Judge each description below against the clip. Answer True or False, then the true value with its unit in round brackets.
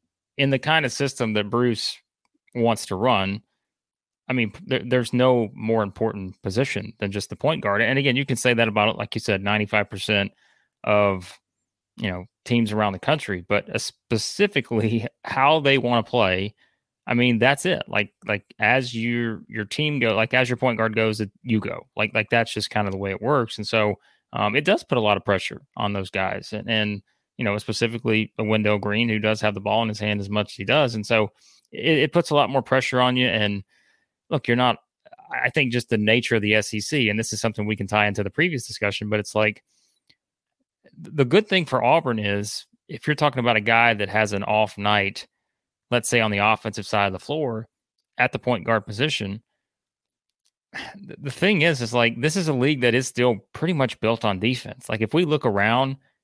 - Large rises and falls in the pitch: False (3.2 semitones)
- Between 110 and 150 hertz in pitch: True (115 Hz)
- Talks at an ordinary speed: False (215 wpm)